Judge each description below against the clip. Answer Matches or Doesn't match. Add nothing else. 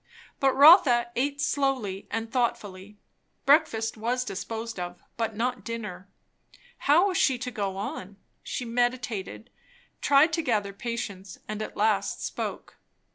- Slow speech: Matches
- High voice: Matches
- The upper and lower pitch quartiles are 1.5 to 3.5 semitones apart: Doesn't match